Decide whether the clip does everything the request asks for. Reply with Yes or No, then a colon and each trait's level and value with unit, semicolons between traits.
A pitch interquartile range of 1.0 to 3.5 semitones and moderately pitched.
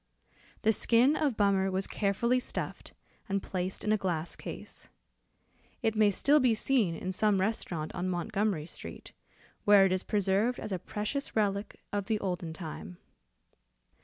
No: average, 2.9 semitones; high, 200 Hz